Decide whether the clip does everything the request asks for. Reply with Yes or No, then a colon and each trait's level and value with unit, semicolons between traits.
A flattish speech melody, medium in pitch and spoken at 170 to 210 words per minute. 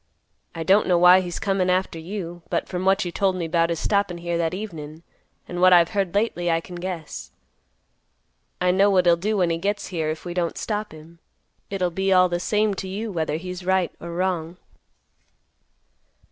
Yes: narrow, 2.2 semitones; medium, 180 Hz; average, 200 wpm